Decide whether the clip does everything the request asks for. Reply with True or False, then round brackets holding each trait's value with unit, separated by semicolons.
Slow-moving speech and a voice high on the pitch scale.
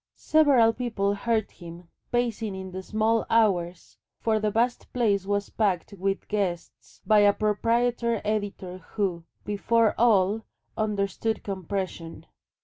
True (125 wpm; 210 Hz)